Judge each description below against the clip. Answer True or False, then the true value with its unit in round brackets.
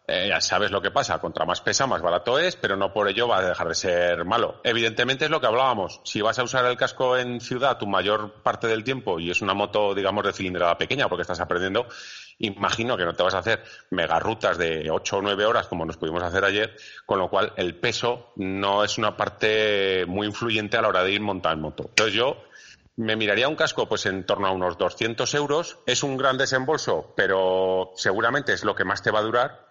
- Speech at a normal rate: False (230 wpm)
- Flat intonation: False (4.5 semitones)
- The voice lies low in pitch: True (105 Hz)